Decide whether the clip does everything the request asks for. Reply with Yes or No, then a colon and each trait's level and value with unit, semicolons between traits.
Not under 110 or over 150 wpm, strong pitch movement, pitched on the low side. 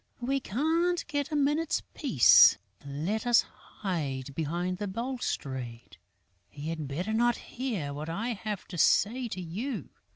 No: average, 140 wpm; wide, 8.5 semitones; high, 205 Hz